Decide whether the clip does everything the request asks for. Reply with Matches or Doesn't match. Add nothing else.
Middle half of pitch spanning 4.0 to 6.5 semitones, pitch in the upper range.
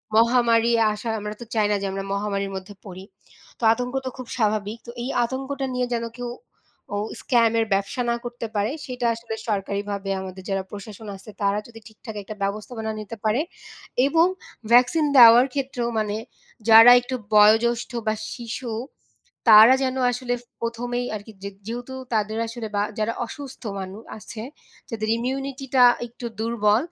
Doesn't match